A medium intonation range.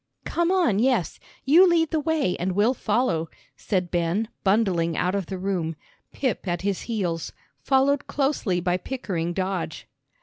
No: wide, 7.1 semitones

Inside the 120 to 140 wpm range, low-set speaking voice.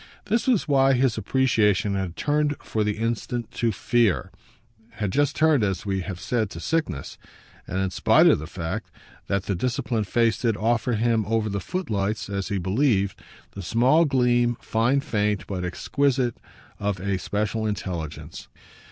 No: average, 160 wpm; low, 110 Hz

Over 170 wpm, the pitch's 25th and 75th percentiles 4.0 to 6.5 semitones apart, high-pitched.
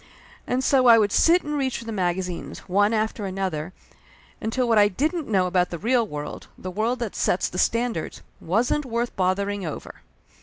Yes: average, 185 wpm; average, 4.7 semitones; high, 210 Hz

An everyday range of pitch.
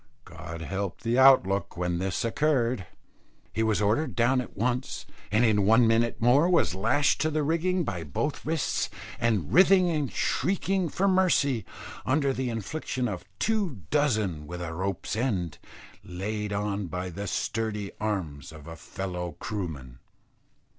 No: wide, 6.9 semitones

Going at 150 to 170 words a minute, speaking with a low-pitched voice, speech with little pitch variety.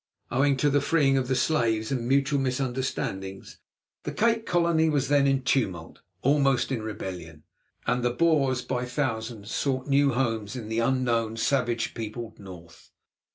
No: average, 155 wpm; low, 125 Hz; average, 3.6 semitones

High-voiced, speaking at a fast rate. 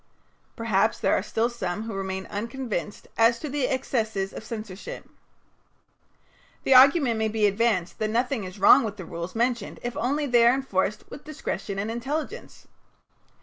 No: high, 225 Hz; average, 160 wpm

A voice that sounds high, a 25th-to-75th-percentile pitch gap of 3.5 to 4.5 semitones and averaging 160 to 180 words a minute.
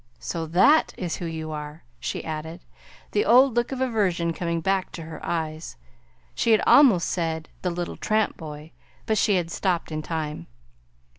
No: medium, 170 Hz; average, 4.2 semitones; average, 170 wpm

